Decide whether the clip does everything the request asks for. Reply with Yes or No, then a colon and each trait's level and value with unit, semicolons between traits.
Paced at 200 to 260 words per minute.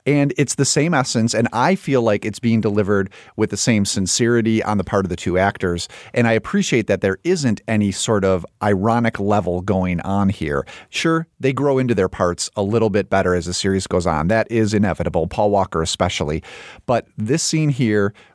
Yes: fast, 205 wpm